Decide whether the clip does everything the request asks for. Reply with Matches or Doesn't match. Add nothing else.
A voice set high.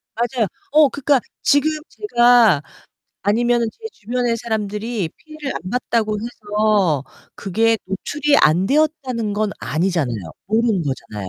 Matches